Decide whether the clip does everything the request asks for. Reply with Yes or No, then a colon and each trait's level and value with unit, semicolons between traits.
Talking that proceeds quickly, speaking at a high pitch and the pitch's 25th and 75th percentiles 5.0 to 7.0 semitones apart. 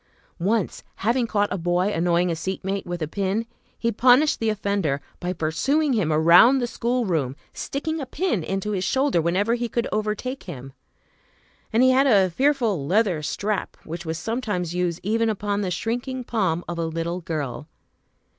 No: average, 175 wpm; high, 200 Hz; wide, 5.4 semitones